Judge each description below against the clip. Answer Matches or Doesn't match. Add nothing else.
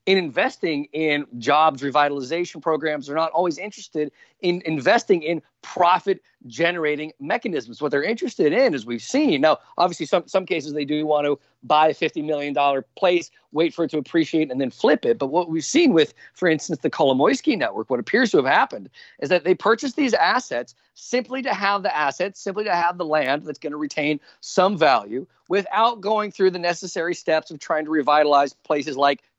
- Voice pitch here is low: Doesn't match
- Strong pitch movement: Doesn't match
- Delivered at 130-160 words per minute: Doesn't match